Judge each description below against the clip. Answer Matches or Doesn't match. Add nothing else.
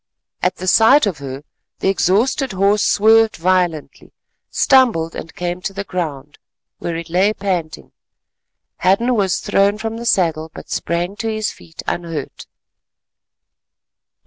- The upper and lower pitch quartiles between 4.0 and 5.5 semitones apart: Matches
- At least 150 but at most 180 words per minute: Doesn't match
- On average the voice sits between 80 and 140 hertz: Doesn't match